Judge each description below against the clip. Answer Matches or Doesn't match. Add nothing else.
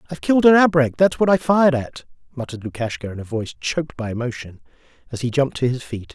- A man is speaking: Matches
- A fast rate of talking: Matches